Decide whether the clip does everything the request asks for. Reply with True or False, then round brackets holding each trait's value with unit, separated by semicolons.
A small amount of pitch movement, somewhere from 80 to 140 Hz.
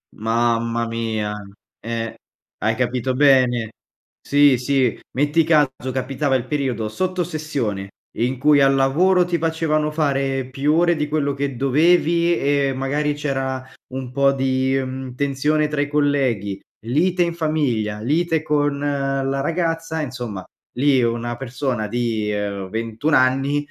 False (3.6 semitones; 135 Hz)